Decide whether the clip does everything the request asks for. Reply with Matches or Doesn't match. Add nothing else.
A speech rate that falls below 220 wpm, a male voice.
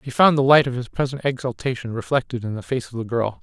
Doesn't match